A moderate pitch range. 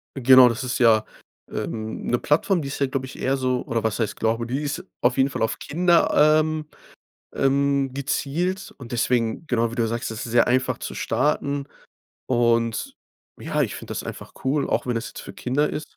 Yes: average, 3.3 semitones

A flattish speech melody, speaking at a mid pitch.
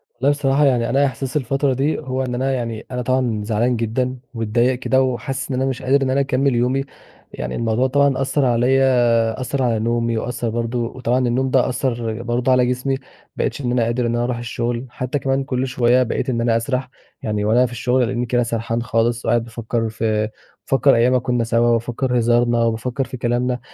No: narrow, 2.0 semitones; low, 125 Hz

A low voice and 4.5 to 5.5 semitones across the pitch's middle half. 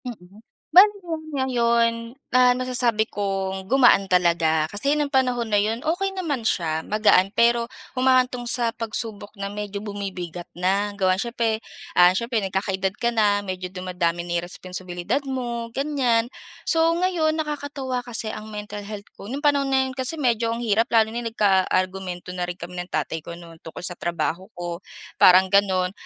No: high, 215 Hz; average, 5.1 semitones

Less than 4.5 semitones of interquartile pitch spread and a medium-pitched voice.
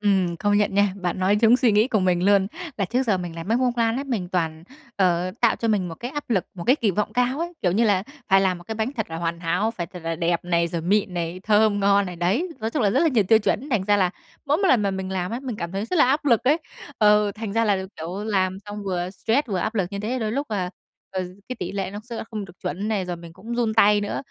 No: average, 3.8 semitones; high, 205 Hz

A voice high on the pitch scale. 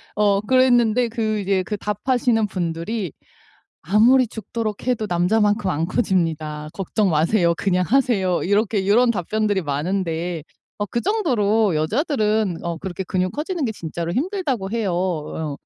Yes: high, 205 Hz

